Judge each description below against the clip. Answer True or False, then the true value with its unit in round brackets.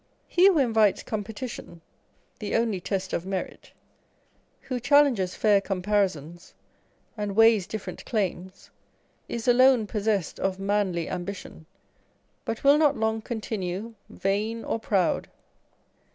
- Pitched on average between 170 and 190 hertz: False (210 Hz)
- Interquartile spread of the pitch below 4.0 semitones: True (3.2 semitones)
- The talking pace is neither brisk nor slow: False (120 wpm)